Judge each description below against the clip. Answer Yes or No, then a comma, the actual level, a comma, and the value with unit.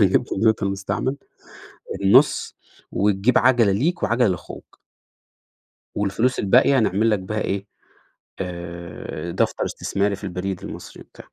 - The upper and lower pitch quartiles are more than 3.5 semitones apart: No, average, 3.2 semitones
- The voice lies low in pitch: Yes, low, 100 Hz